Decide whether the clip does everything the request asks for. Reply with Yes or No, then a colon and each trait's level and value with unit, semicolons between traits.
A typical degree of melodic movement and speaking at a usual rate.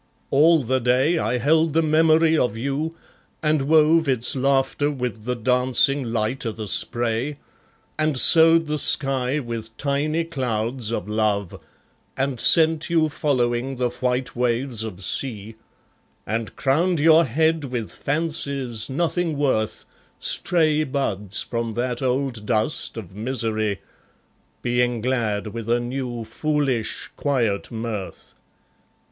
No: average, 4.6 semitones; slow, 130 wpm